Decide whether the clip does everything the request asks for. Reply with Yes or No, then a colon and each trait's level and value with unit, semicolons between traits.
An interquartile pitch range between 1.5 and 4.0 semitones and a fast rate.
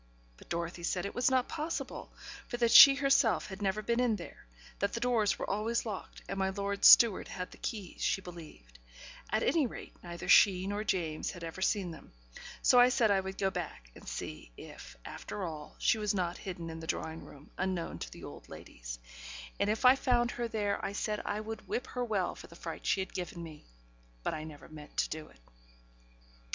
No: average, 4.7 semitones; fast, 210 wpm